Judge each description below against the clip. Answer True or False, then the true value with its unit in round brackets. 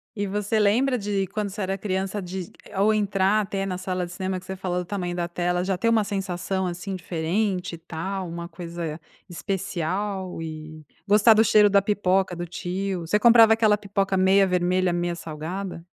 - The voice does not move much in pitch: True (2.3 semitones)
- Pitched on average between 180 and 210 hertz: True (190 Hz)